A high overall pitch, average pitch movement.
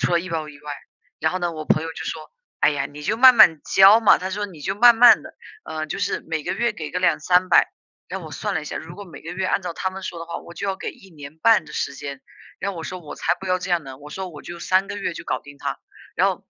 No: medium, 175 Hz; average, 3.7 semitones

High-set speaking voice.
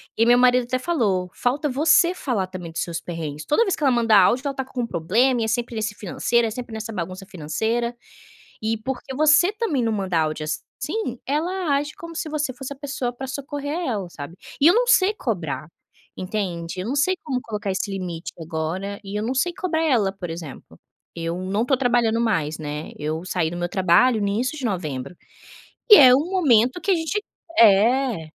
Yes: high, 230 Hz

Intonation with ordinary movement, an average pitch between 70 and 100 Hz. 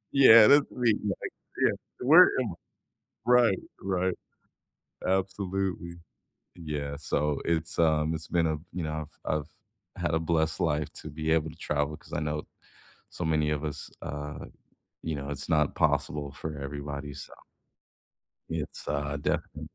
Yes: average, 3.3 semitones; very low, 80 Hz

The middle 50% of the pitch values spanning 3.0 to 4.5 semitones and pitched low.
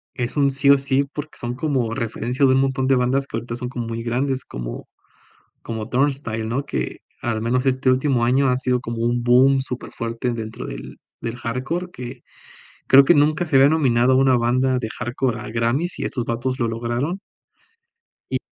No: narrow, 2.6 semitones; low, 125 Hz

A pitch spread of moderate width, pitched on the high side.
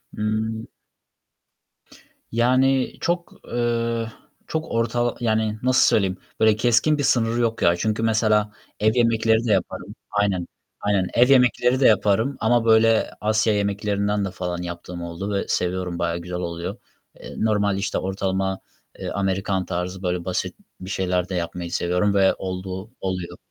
No: average, 3.6 semitones; low, 105 Hz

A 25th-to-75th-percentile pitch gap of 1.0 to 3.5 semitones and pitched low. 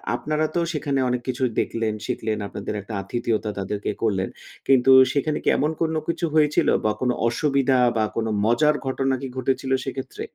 No: average, 4.1 semitones; low, 130 Hz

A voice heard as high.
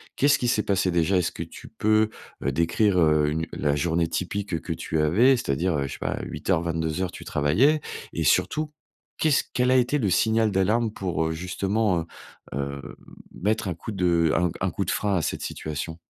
No: very low, 90 Hz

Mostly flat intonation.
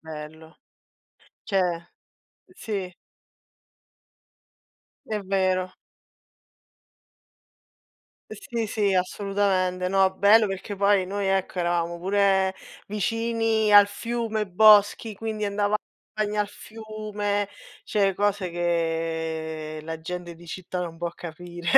No: average, 3.2 semitones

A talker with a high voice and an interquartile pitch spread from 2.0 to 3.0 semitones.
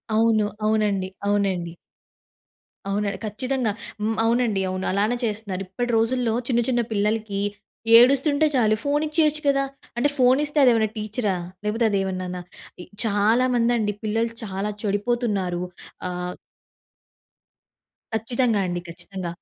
No: high, 215 Hz; average, 3.5 semitones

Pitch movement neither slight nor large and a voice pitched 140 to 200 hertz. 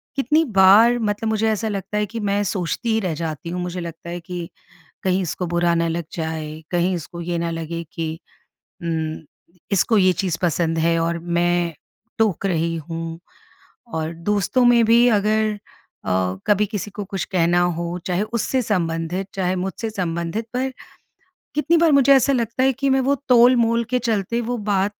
Yes: average, 5.0 semitones; high, 190 Hz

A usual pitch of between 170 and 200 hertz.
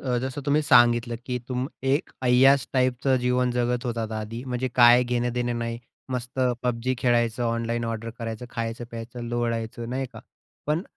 No: low, 120 Hz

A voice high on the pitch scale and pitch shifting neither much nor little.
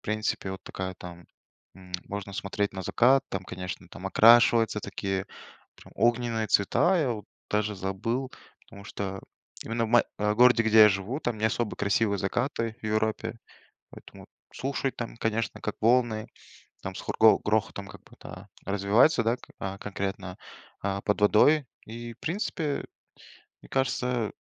No: low, 110 Hz; average, 3.2 semitones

